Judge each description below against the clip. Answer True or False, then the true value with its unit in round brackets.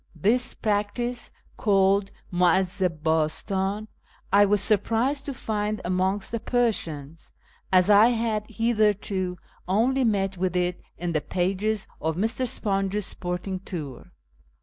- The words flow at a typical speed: False (120 wpm)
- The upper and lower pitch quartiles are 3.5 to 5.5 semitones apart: False (3.1 semitones)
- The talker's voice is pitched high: True (200 Hz)